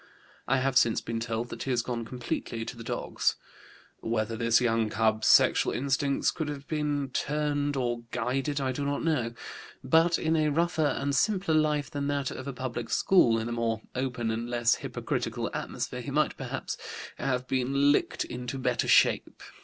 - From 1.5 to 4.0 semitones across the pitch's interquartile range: Yes, average, 3.5 semitones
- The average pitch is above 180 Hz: No, low, 130 Hz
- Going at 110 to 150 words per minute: No, average, 180 wpm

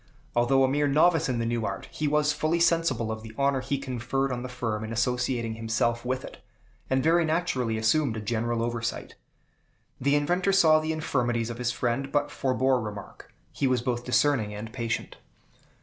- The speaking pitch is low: Yes, low, 125 Hz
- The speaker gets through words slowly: No, average, 185 wpm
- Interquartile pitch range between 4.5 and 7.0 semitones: No, average, 3.9 semitones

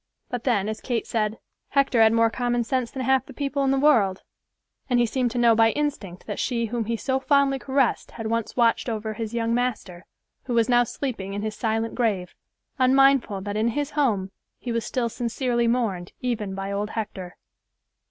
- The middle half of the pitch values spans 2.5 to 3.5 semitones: Yes, average, 2.9 semitones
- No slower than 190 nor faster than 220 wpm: Yes, average, 200 wpm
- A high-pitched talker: Yes, high, 235 Hz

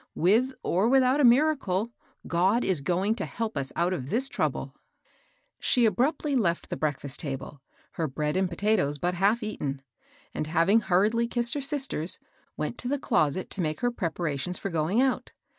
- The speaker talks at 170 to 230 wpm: Yes, average, 175 wpm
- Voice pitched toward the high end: Yes, high, 195 Hz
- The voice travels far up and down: Yes, wide, 6.9 semitones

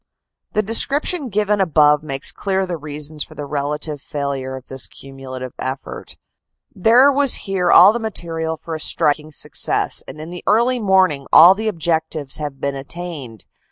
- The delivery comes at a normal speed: Yes, average, 160 wpm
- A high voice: No, medium, 160 Hz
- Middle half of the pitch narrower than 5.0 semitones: No, wide, 5.6 semitones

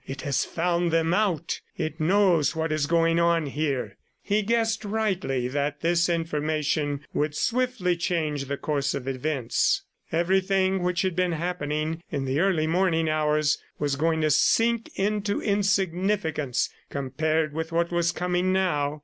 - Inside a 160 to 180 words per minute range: No, average, 150 wpm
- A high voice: No, medium, 165 Hz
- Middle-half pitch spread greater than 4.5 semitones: No, average, 3.7 semitones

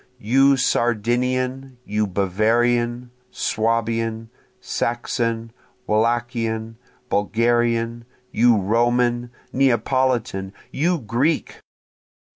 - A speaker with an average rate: No, slow, 65 wpm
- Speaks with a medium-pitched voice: No, low, 120 Hz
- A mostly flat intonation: Yes, narrow, 1.5 semitones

